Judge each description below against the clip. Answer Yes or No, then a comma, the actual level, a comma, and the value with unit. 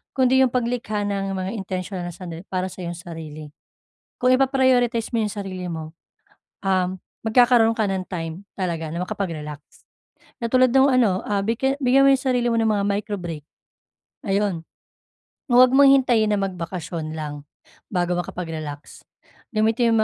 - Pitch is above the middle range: Yes, high, 200 Hz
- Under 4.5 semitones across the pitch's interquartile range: No, wide, 5.5 semitones